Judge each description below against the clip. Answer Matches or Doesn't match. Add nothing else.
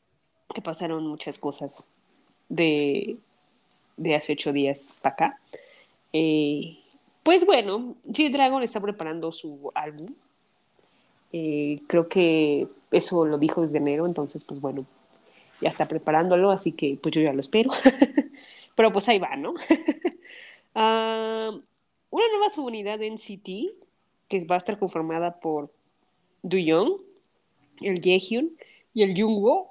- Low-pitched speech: Doesn't match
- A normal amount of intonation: Doesn't match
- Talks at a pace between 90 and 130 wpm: Matches